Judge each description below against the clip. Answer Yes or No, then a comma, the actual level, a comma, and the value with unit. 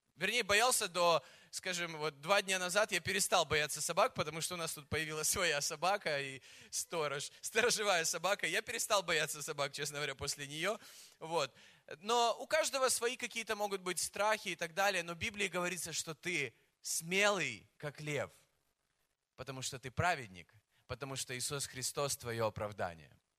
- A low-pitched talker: No, medium, 165 Hz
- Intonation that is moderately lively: No, wide, 6.1 semitones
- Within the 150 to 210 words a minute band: Yes, fast, 160 wpm